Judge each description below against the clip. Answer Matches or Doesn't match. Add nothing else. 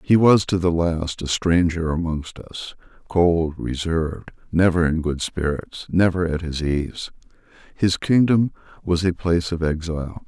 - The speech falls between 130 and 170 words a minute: Matches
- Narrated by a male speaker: Matches